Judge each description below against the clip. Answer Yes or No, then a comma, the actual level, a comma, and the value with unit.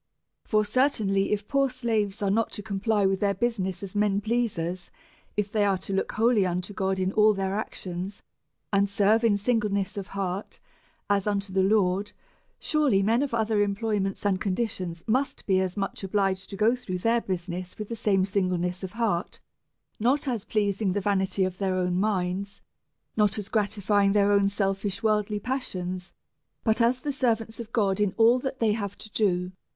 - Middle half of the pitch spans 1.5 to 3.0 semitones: Yes, narrow, 2.5 semitones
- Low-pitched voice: No, high, 200 Hz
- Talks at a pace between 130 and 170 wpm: No, average, 185 wpm